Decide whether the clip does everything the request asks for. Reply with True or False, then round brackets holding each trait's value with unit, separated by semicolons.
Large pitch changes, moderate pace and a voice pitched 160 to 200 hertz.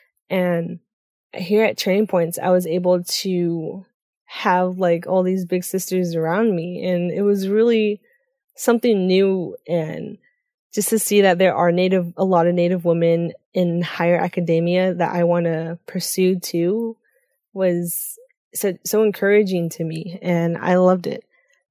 False (3.0 semitones; 150 wpm; 185 Hz)